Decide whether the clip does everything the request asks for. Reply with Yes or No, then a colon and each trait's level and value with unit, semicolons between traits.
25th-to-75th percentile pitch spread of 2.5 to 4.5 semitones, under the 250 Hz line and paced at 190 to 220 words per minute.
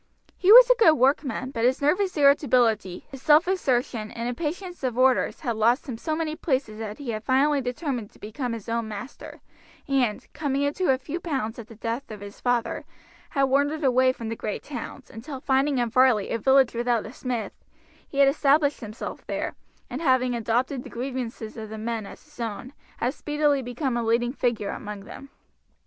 No: average, 3.7 semitones; very high, 255 Hz; average, 195 wpm